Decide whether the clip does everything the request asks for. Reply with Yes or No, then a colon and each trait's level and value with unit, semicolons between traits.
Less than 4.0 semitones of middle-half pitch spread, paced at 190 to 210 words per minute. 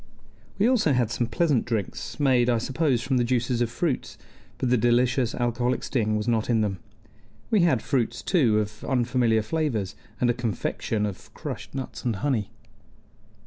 No: average, 2.8 semitones; average, 170 wpm